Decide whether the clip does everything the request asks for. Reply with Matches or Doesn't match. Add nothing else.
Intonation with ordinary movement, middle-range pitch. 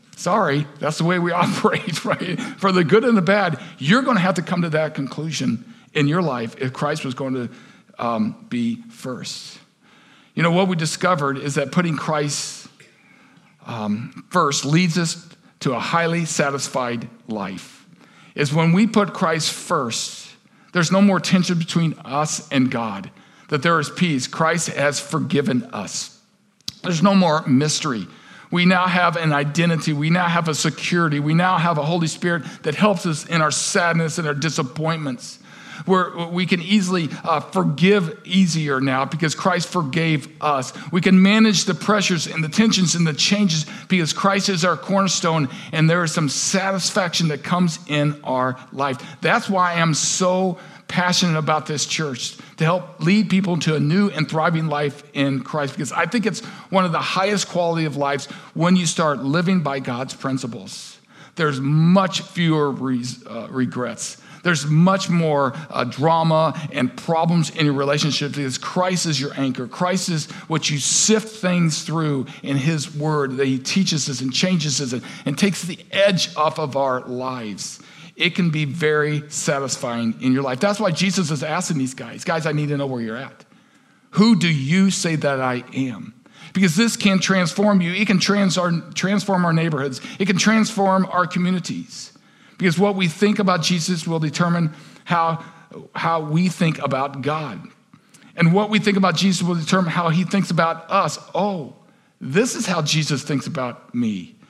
Matches